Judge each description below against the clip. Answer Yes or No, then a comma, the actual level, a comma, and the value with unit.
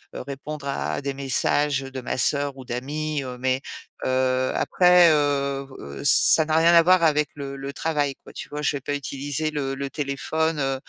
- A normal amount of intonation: No, narrow, 2.0 semitones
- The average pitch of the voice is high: No, medium, 140 Hz